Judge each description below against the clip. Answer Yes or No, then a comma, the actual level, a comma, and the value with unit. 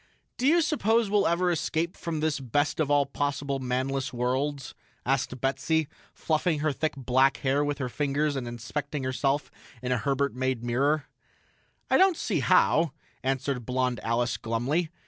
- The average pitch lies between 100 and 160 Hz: Yes, medium, 140 Hz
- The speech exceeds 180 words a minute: No, average, 160 wpm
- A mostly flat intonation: No, average, 3.2 semitones